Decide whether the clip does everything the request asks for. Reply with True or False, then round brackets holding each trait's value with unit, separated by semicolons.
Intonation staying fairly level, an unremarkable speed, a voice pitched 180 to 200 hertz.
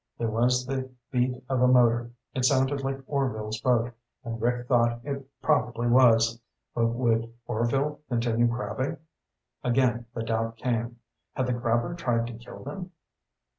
False (1.9 semitones; 150 wpm; 120 Hz)